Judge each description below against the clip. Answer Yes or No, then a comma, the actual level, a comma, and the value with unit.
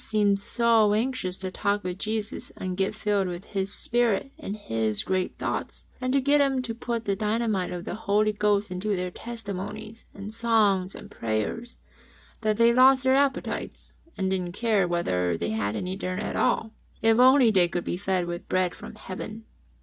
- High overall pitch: Yes, high, 205 Hz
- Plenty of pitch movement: No, average, 3.7 semitones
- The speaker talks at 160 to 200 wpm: Yes, average, 190 wpm